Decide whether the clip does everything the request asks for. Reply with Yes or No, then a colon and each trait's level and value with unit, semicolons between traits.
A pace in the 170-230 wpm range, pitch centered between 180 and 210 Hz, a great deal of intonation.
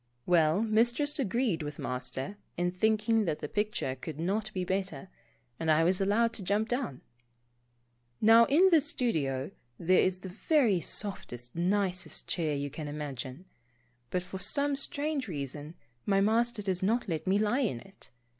No: average, 160 wpm; high, 190 Hz; wide, 5.9 semitones